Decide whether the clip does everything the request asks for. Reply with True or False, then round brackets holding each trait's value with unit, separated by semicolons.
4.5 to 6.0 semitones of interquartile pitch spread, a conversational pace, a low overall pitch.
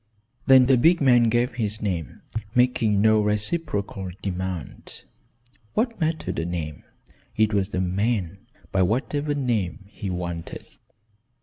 False (5.1 semitones; 125 wpm; 105 Hz)